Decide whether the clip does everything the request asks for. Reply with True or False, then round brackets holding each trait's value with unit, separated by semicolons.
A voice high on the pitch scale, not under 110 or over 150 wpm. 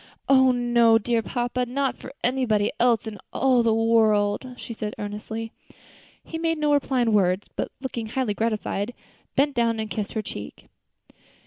False (230 Hz; 160 wpm)